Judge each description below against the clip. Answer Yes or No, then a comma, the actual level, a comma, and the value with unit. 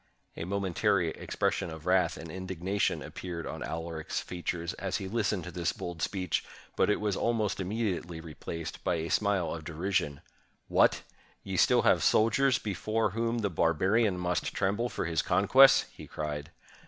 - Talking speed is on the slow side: No, average, 160 wpm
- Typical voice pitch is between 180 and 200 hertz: No, very low, 90 Hz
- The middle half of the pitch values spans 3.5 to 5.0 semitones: Yes, average, 3.9 semitones